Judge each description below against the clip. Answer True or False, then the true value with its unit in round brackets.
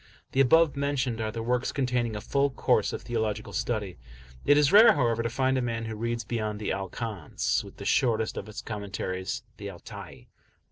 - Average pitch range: True (3.4 semitones)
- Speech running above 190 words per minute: True (200 wpm)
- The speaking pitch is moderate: False (115 Hz)